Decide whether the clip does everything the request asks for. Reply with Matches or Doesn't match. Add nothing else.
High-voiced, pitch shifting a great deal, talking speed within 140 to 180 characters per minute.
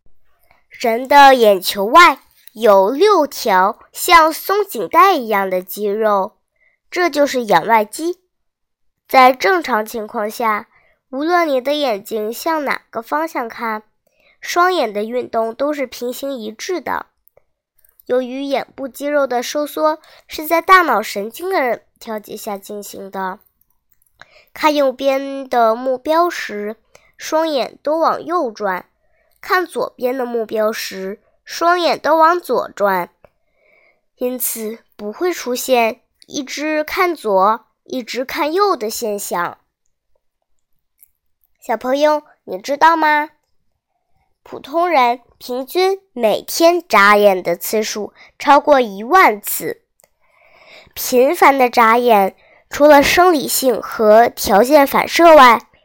Matches